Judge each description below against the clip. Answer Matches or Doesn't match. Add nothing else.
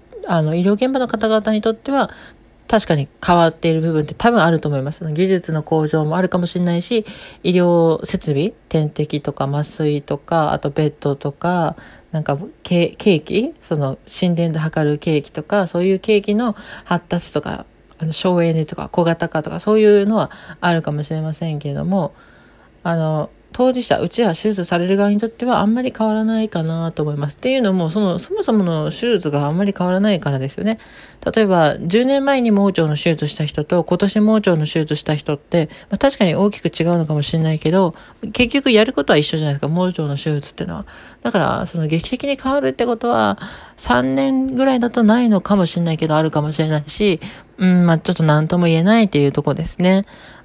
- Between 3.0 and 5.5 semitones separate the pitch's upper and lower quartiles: Matches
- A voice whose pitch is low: Doesn't match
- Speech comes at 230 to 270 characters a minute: Doesn't match